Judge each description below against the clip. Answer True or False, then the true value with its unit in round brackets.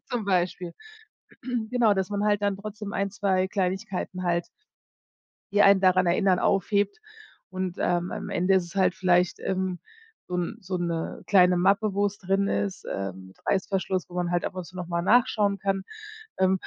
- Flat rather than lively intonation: True (1.9 semitones)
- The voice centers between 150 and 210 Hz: True (190 Hz)